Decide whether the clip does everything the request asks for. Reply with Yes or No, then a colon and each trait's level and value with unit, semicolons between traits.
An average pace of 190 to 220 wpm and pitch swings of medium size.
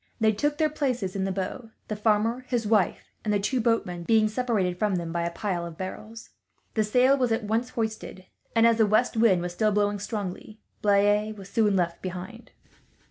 Yes: average, 200 wpm; average, 3.1 semitones